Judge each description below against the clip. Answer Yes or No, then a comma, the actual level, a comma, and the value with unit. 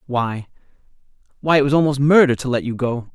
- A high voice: No, low, 135 Hz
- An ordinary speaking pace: Yes, average, 155 wpm